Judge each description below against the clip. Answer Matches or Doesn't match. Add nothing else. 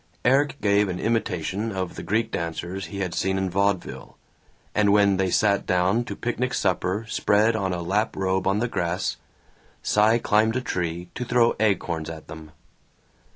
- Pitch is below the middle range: Matches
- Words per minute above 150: Matches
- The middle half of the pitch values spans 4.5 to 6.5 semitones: Doesn't match